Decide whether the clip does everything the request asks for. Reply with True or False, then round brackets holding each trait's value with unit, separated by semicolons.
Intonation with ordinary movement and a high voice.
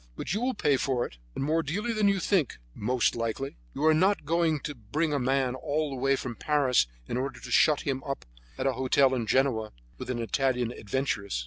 False (3.7 semitones; 135 Hz)